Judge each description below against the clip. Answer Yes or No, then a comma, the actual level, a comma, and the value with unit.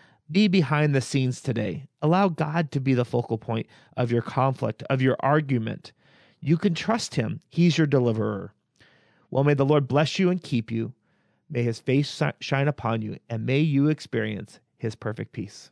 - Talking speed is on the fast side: No, average, 180 wpm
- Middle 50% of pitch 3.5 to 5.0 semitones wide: Yes, average, 4.5 semitones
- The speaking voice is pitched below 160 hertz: Yes, low, 135 Hz